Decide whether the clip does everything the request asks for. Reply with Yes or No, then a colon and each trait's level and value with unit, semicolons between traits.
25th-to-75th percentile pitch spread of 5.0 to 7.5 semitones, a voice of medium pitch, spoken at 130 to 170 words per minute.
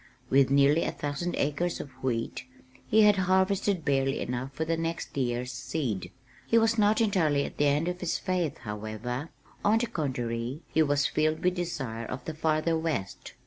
No: average, 5.3 semitones; medium, 150 Hz; average, 180 wpm